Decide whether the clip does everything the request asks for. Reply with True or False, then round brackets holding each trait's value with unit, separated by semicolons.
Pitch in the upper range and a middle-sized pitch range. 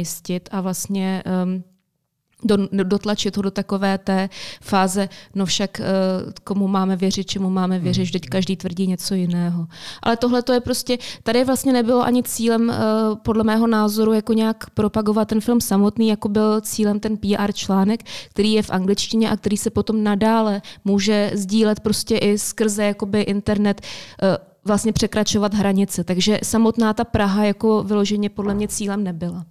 False (205 Hz; 2.3 semitones)